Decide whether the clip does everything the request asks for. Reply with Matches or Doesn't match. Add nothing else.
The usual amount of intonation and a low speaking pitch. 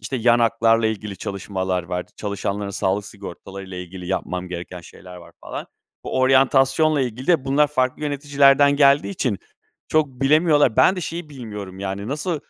Doesn't match